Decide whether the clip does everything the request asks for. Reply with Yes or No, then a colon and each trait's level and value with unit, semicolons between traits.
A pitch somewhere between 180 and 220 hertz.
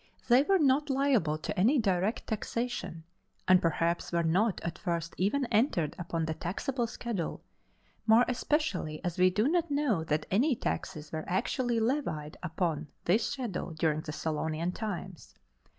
Yes: high, 190 Hz